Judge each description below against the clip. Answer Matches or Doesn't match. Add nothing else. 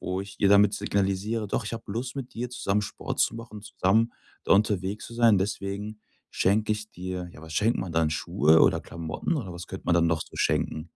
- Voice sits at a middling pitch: Doesn't match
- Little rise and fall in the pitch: Doesn't match